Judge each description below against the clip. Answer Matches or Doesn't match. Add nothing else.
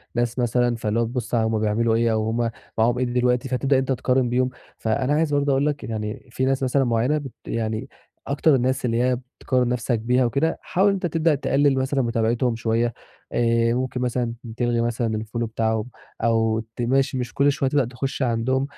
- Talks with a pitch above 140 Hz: Doesn't match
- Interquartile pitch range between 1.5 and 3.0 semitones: Matches